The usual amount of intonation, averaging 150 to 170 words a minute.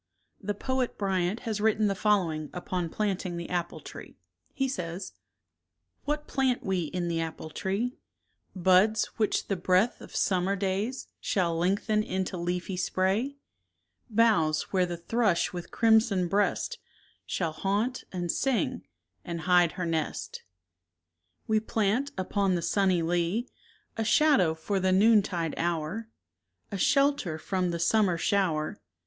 No: average, 3.9 semitones; average, 140 wpm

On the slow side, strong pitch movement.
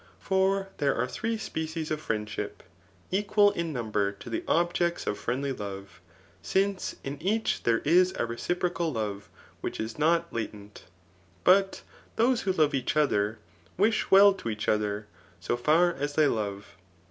No: average, 160 wpm; wide, 9.0 semitones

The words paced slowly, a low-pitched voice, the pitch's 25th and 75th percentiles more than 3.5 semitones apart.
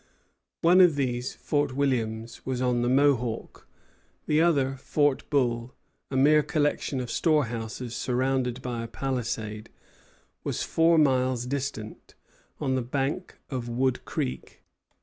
No: slow, 130 wpm; low, 130 Hz; average, 2.9 semitones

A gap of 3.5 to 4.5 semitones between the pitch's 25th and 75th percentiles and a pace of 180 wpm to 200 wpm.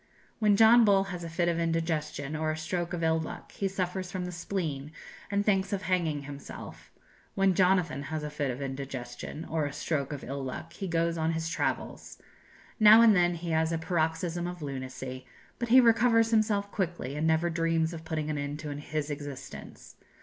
Yes: average, 3.9 semitones; average, 195 wpm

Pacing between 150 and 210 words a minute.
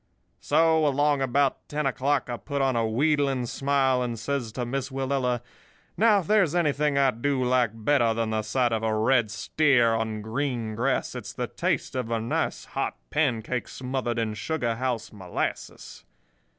Yes: average, 170 wpm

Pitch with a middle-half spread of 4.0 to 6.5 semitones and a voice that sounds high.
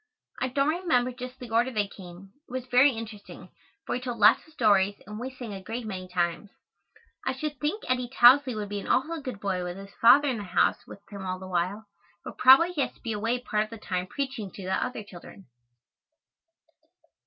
Yes: average, 4.6 semitones; high, 225 Hz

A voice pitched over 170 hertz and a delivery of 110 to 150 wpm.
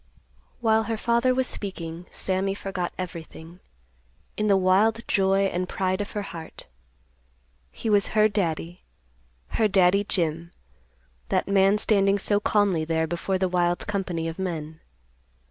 Yes: high, 190 Hz; average, 140 wpm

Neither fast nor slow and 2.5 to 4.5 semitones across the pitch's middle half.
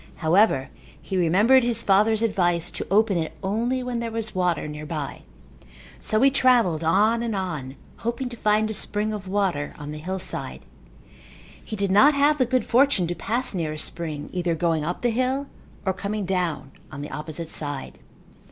No: average, 180 wpm; wide, 5.6 semitones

